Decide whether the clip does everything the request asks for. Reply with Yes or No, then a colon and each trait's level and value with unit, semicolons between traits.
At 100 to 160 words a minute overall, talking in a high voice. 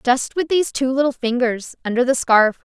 No: average, 200 wpm; very high, 255 Hz